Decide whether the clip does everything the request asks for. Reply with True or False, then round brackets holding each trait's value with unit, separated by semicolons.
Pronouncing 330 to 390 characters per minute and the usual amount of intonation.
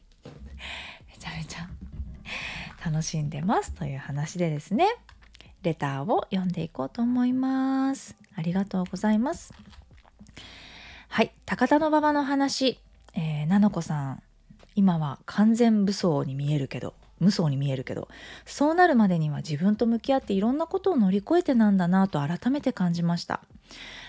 False (335 characters per minute; 7.7 semitones)